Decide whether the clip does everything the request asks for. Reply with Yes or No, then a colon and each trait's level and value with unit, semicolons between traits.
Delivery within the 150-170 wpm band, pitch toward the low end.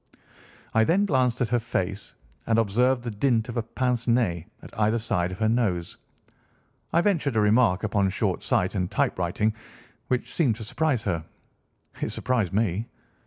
Yes: average, 165 wpm; low, 115 Hz